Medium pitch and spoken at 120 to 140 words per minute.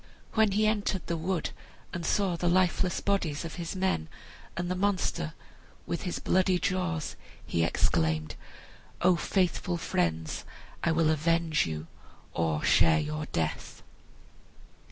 Yes: medium, 170 Hz; slow, 135 wpm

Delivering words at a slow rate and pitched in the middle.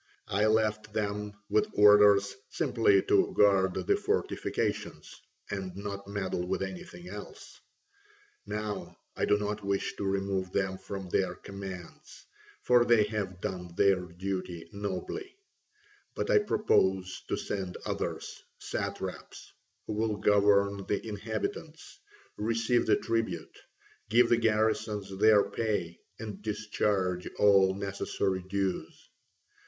No: slow, 120 wpm; low, 100 Hz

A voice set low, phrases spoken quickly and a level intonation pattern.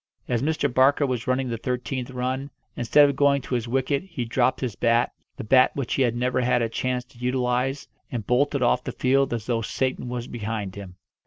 Yes: low, 125 Hz; fast, 215 wpm; narrow, 2.0 semitones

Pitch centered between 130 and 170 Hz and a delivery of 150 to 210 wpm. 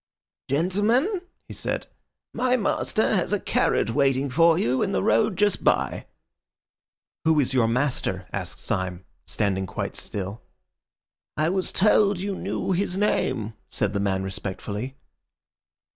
No: medium, 140 Hz; slow, 135 wpm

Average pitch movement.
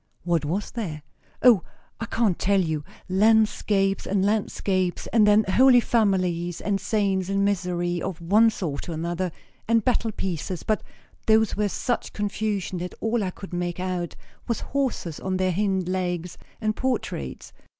Yes: average, 3.4 semitones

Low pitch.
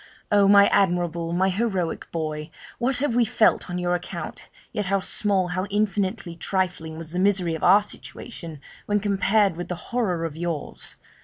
No: medium, 185 Hz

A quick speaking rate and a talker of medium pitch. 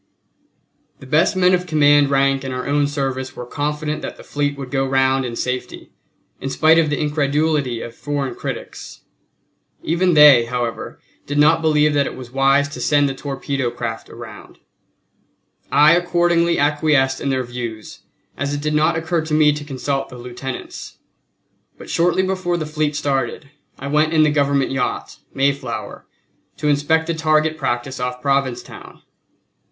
No: average, 165 wpm; medium, 145 Hz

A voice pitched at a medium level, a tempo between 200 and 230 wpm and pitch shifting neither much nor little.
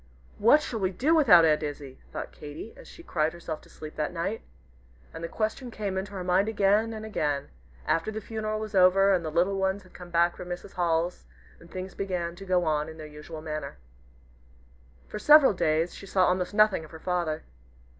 Yes: medium, 180 Hz; fast, 205 wpm; average, 4.1 semitones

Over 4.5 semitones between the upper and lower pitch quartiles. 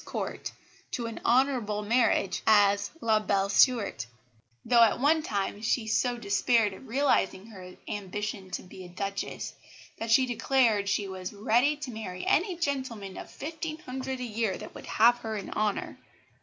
No: average, 4.0 semitones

